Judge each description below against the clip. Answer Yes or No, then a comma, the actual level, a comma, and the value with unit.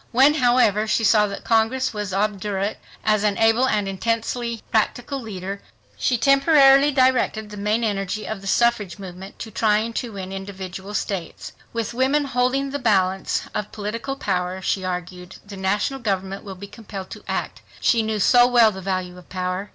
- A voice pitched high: Yes, high, 210 Hz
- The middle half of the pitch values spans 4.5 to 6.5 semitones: No, average, 3.7 semitones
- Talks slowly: No, average, 175 wpm